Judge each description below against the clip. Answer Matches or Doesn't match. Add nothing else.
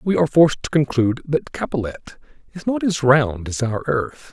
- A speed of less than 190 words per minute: Doesn't match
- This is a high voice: Doesn't match